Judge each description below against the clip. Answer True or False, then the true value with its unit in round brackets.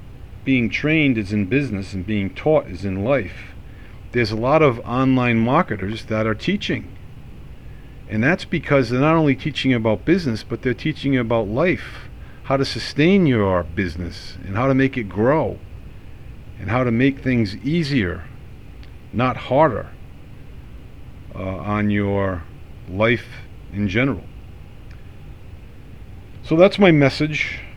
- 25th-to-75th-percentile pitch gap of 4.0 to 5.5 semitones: True (5.0 semitones)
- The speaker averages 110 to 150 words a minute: True (135 wpm)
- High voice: False (115 Hz)